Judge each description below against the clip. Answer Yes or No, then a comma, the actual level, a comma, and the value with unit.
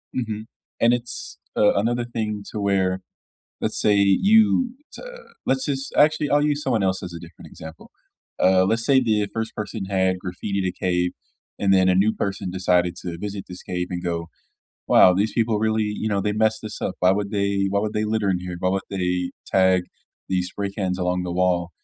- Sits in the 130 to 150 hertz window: No, low, 100 Hz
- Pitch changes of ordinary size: Yes, average, 3.1 semitones